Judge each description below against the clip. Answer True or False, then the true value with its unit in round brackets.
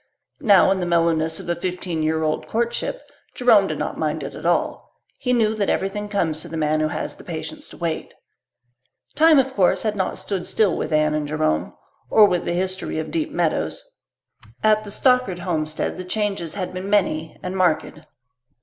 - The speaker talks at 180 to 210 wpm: True (190 wpm)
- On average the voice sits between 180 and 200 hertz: True (185 Hz)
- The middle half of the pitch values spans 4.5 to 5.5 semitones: True (4.9 semitones)